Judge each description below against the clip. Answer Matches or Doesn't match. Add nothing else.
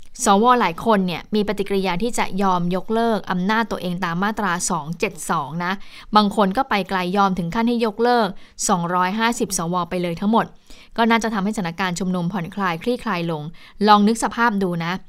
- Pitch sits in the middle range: Doesn't match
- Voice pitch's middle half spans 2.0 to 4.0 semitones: Matches